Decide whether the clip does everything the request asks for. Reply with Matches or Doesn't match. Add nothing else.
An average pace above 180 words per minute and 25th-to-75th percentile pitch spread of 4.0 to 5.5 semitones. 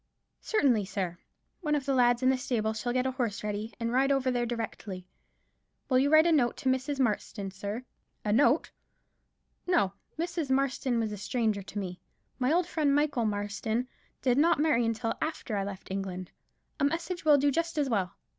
Matches